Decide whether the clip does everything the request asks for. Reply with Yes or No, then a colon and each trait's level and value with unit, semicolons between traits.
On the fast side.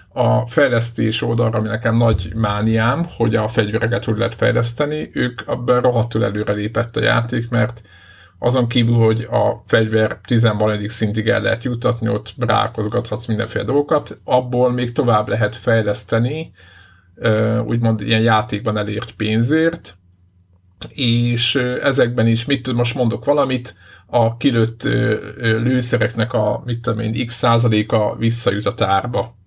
No: average, 125 wpm